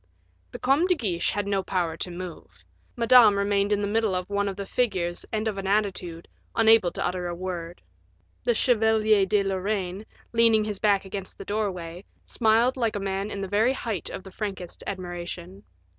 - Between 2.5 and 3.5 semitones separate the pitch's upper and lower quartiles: Yes, average, 3.0 semitones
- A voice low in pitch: No, high, 200 Hz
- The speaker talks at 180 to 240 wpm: Yes, average, 190 wpm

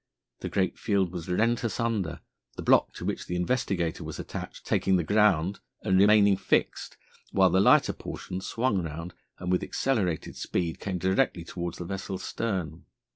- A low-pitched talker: Yes, very low, 95 Hz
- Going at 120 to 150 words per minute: No, average, 165 wpm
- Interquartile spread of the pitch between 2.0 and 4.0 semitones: Yes, average, 2.8 semitones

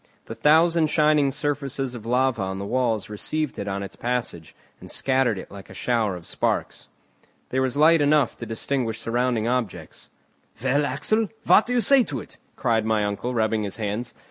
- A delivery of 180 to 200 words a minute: Yes, average, 185 wpm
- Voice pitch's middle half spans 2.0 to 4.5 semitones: No, average, 4.9 semitones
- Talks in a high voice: No, low, 125 Hz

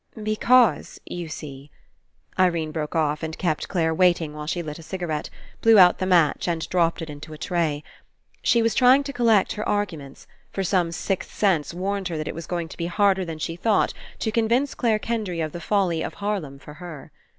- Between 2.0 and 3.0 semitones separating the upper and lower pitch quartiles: No, average, 4.4 semitones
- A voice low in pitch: No, medium, 175 Hz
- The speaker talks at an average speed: No, fast, 210 wpm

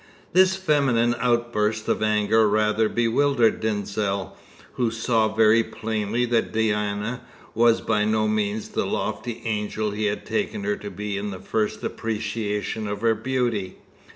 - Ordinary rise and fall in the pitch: No, narrow, 1.9 semitones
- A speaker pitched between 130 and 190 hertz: No, low, 110 Hz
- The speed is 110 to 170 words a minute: Yes, average, 145 wpm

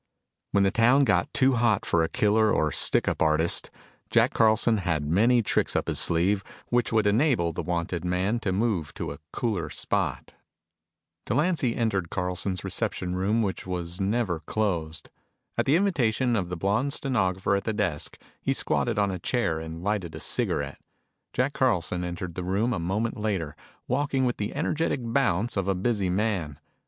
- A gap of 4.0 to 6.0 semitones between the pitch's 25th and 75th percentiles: Yes, average, 4.8 semitones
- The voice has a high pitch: No, low, 100 Hz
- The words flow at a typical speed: Yes, average, 175 wpm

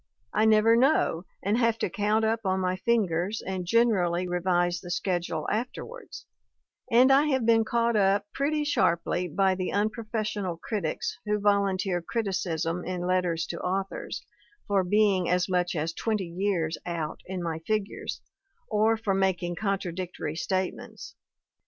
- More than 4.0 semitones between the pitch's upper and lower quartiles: No, average, 3.5 semitones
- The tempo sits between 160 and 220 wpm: No, average, 145 wpm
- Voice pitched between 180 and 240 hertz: Yes, high, 190 Hz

